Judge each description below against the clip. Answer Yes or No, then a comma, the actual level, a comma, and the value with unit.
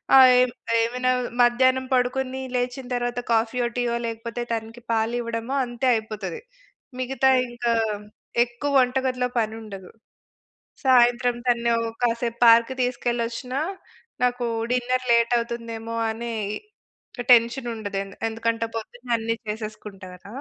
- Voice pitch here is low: No, high, 240 Hz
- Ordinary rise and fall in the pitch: No, narrow, 1.6 semitones